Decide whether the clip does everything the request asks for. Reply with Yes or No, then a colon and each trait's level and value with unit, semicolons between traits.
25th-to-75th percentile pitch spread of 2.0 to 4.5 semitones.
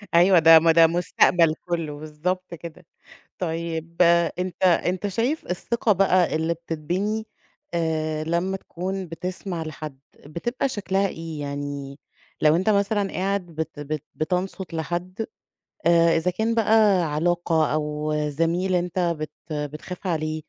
Yes: average, 3.0 semitones